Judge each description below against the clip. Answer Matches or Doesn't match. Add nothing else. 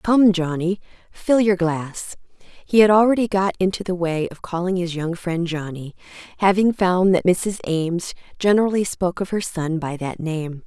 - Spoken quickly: Doesn't match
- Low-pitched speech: Doesn't match